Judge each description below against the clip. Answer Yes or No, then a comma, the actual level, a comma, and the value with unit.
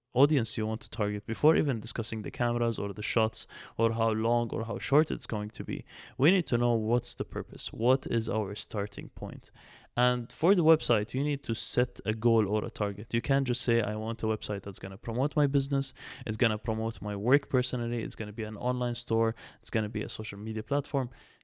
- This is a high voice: No, low, 115 Hz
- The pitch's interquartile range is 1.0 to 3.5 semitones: Yes, average, 2.9 semitones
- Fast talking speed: Yes, fast, 235 wpm